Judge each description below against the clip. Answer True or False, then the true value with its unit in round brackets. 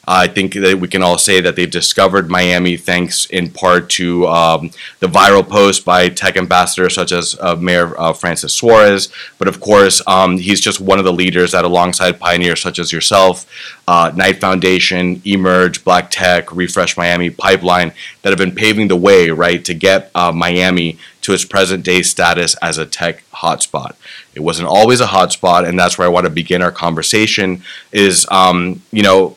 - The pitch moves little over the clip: True (1.4 semitones)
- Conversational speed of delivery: True (185 wpm)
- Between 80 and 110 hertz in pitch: True (90 Hz)